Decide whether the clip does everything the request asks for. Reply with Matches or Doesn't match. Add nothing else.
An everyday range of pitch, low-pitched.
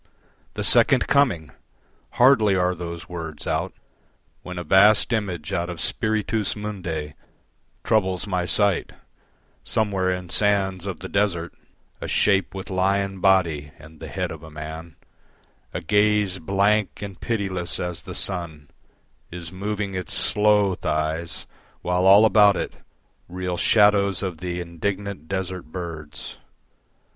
Matches